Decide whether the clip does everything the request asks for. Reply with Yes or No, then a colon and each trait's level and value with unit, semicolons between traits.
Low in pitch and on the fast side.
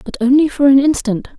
No: very high, 270 Hz; fast, 215 wpm